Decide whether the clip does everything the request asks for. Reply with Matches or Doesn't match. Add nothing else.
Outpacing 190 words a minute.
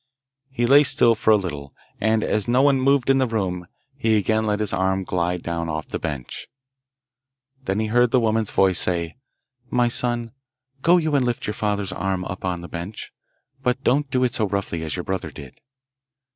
Matches